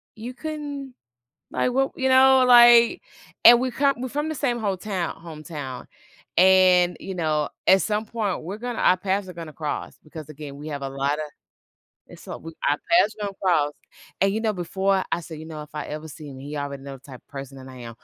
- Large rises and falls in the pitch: Yes, wide, 7.8 semitones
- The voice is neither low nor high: Yes, medium, 180 Hz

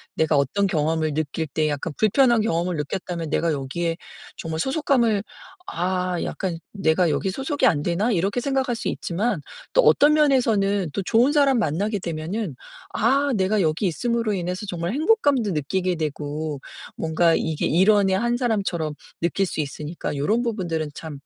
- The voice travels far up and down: Yes, wide, 6.2 semitones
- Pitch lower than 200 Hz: Yes, medium, 185 Hz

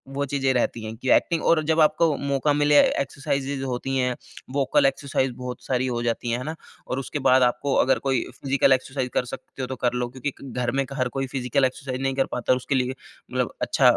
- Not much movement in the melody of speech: Yes, narrow, 1.8 semitones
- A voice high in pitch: No, low, 130 Hz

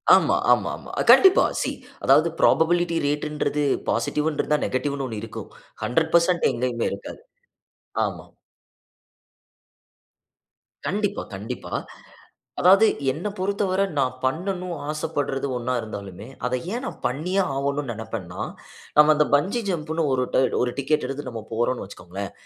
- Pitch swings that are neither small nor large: No, wide, 5.7 semitones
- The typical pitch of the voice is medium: Yes, medium, 150 Hz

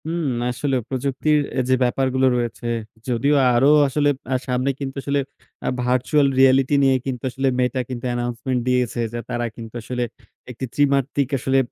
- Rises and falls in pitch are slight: Yes, narrow, 1.9 semitones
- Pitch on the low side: Yes, low, 130 Hz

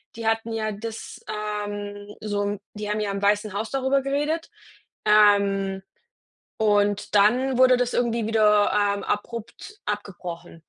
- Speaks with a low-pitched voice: No, high, 210 Hz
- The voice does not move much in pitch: Yes, narrow, 2.0 semitones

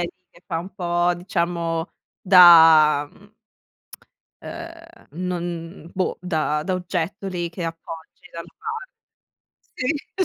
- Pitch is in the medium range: Yes, medium, 175 Hz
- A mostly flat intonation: Yes, narrow, 2.1 semitones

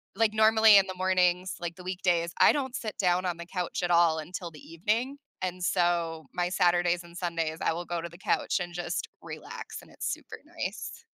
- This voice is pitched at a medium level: Yes, medium, 175 Hz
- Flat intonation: Yes, narrow, 1.6 semitones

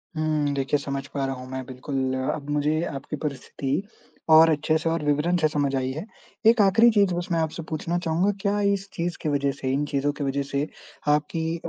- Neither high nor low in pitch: Yes, medium, 150 Hz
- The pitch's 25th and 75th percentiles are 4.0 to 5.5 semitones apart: No, average, 3.2 semitones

